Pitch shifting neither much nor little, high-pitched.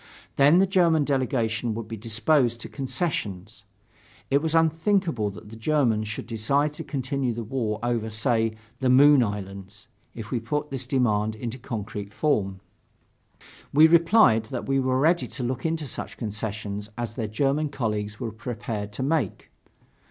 No: average, 4.8 semitones; low, 120 Hz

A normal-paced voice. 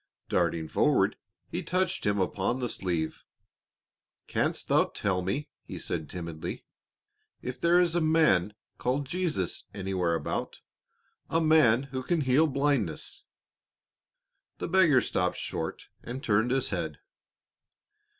No: slow, 125 wpm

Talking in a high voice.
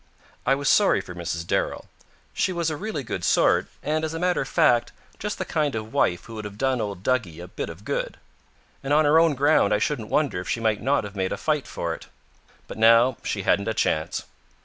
No: low, 120 Hz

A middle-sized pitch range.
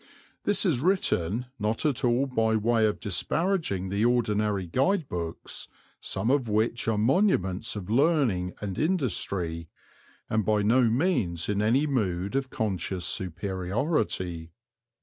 No: wide, 5.9 semitones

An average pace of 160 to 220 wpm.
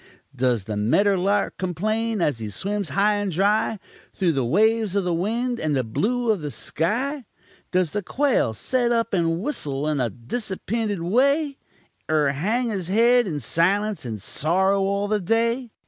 Yes: average, 170 wpm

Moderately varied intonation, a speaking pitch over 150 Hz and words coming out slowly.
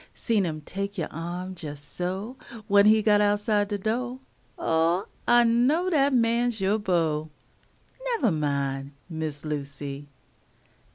No: wide, 6.4 semitones; high, 190 Hz; slow, 130 wpm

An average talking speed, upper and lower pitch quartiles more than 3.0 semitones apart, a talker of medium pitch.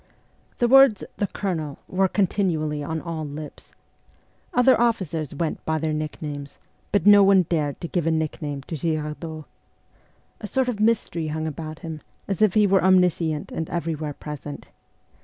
Yes: average, 165 wpm; average, 4.2 semitones; medium, 160 Hz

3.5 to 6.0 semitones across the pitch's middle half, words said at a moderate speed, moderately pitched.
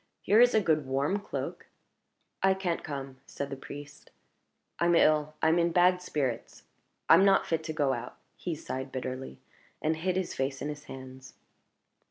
Yes: average, 4.6 semitones; average, 175 wpm; medium, 155 Hz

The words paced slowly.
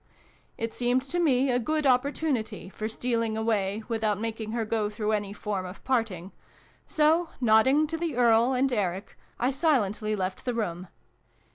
No: average, 160 wpm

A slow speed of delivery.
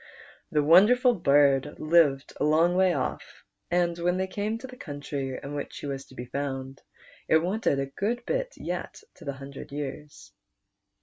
No: average, 175 wpm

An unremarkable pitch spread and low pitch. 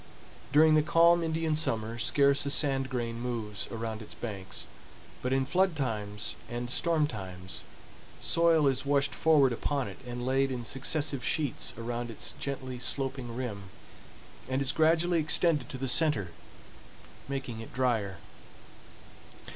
Yes: average, 4.3 semitones; low, 130 Hz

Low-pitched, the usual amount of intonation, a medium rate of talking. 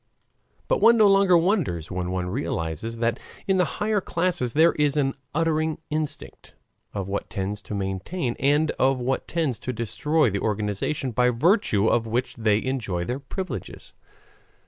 No: low, 125 Hz; wide, 7.3 semitones; average, 160 wpm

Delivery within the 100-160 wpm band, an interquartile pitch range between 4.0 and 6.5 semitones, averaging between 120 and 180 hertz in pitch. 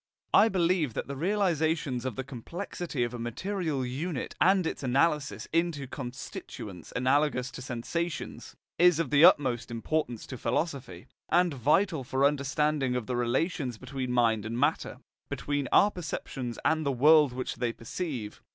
Yes: average, 155 wpm; average, 4.7 semitones; medium, 140 Hz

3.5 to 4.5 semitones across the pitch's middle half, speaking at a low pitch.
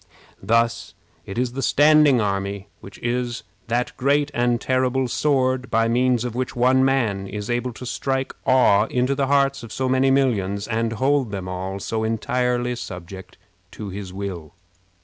Yes: average, 4.2 semitones; low, 120 Hz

